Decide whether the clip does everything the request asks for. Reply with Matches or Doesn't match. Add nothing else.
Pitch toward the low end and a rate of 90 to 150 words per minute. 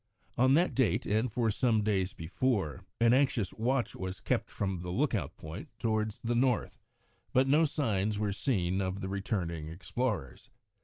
Doesn't match